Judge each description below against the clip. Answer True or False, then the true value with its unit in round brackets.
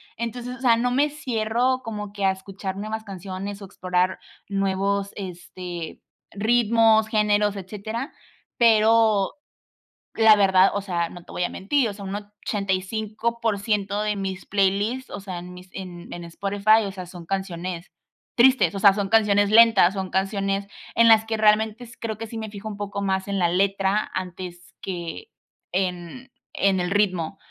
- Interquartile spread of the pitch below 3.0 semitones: True (2.5 semitones)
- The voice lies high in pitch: True (200 Hz)